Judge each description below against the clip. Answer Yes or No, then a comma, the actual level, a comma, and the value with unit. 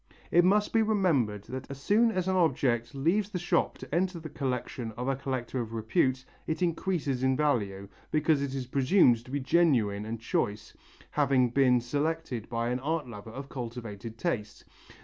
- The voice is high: No, low, 130 Hz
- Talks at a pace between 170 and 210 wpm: Yes, average, 180 wpm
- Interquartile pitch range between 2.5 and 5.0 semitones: No, wide, 5.5 semitones